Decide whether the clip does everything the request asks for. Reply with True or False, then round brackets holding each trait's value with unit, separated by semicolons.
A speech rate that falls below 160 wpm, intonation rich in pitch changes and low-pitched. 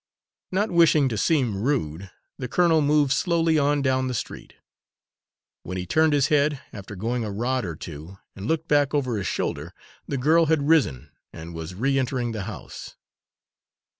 False (170 wpm; 6.8 semitones; 130 Hz)